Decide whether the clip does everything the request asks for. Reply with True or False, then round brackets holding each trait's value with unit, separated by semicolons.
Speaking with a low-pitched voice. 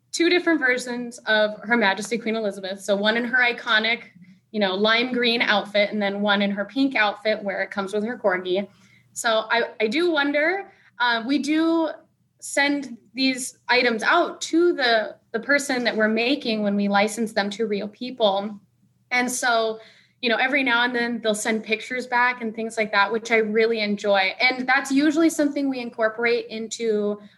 False (230 Hz)